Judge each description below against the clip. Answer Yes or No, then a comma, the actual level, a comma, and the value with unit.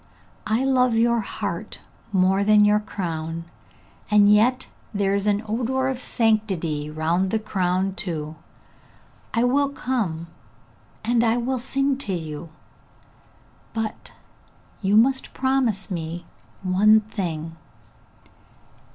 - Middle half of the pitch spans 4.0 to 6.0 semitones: Yes, average, 4.7 semitones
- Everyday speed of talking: No, slow, 115 wpm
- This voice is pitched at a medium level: No, high, 210 Hz